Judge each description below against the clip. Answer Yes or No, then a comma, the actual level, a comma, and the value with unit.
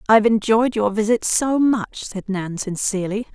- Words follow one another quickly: No, average, 160 wpm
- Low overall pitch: No, high, 215 Hz